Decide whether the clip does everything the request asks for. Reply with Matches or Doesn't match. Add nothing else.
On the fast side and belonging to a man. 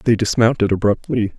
Doesn't match